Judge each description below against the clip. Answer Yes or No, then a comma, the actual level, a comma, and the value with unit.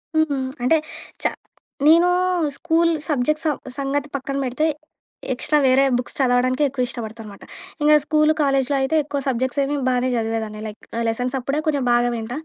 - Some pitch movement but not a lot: Yes, average, 3.2 semitones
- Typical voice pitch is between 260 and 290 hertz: Yes, very high, 265 Hz